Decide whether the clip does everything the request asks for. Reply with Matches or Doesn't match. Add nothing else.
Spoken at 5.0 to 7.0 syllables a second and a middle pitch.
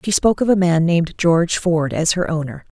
Matches